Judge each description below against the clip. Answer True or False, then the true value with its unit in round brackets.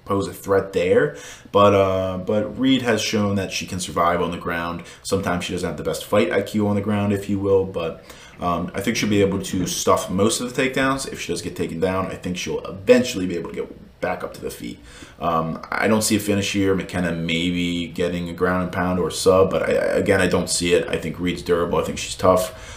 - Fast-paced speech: True (250 wpm)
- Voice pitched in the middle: False (95 Hz)